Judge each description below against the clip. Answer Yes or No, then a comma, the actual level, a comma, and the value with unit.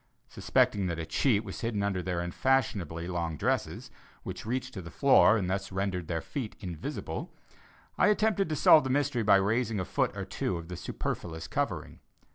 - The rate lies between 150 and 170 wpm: No, average, 185 wpm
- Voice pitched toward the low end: Yes, low, 100 Hz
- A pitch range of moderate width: No, wide, 6.2 semitones